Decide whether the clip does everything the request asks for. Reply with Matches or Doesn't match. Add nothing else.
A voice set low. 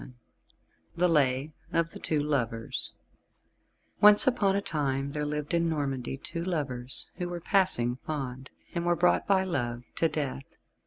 Doesn't match